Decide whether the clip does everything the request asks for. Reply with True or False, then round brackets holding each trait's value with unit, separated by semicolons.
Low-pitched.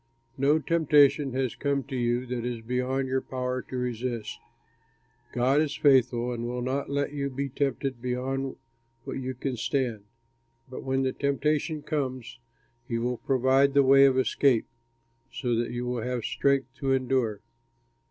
True (130 Hz)